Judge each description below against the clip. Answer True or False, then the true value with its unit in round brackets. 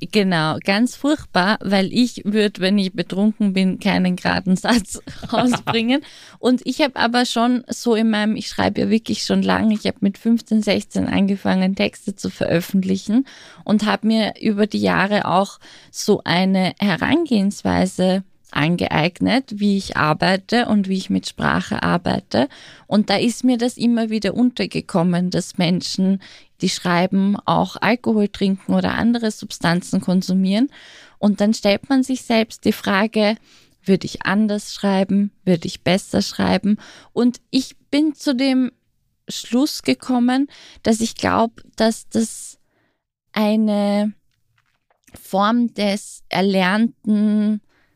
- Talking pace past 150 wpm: False (135 wpm)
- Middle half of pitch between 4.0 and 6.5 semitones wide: False (3.2 semitones)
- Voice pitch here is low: False (210 Hz)